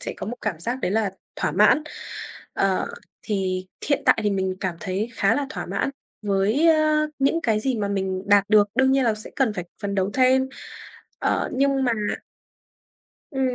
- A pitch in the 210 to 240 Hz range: Yes, high, 215 Hz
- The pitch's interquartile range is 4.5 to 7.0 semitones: Yes, average, 5.3 semitones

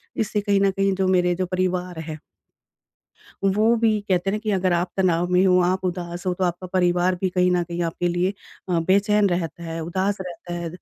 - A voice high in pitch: No, medium, 180 Hz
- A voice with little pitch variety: Yes, narrow, 1.7 semitones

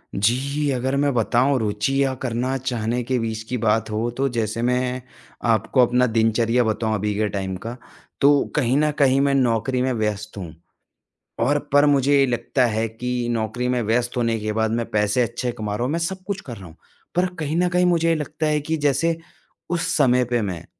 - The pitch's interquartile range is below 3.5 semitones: No, average, 3.8 semitones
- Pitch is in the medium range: No, low, 125 Hz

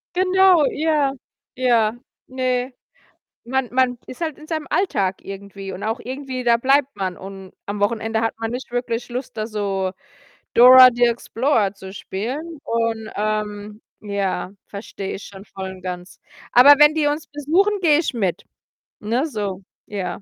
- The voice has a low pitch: No, high, 230 Hz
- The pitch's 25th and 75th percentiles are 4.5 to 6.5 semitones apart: Yes, average, 5.2 semitones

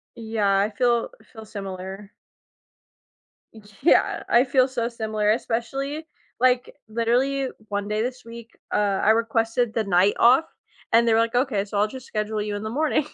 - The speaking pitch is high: Yes, high, 225 Hz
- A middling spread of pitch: Yes, average, 3.0 semitones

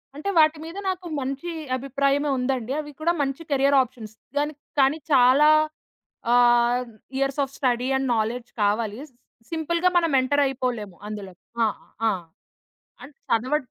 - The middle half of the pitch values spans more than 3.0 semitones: Yes, average, 3.5 semitones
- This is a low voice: No, very high, 270 Hz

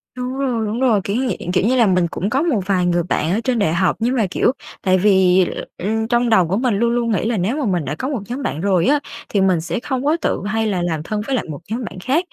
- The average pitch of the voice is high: Yes, high, 215 Hz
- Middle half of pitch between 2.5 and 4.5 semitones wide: No, average, 5.1 semitones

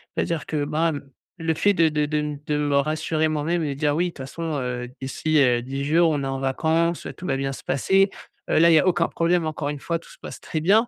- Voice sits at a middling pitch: Yes, medium, 155 Hz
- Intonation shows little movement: No, average, 3.0 semitones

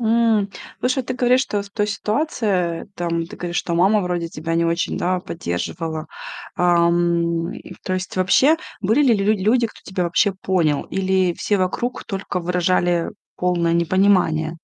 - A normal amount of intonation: Yes, average, 3.4 semitones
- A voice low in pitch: No, medium, 185 Hz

